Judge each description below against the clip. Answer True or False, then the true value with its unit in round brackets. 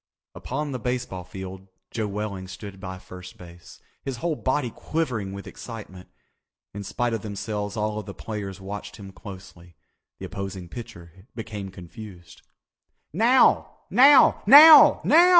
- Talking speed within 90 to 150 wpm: True (135 wpm)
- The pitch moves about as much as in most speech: True (4.4 semitones)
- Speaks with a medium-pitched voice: False (100 Hz)